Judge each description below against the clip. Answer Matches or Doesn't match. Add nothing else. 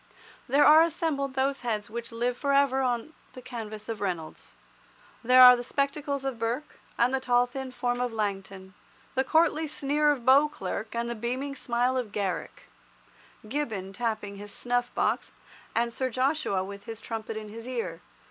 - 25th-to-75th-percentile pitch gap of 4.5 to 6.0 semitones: Doesn't match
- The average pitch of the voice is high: Matches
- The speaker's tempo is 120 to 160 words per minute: Doesn't match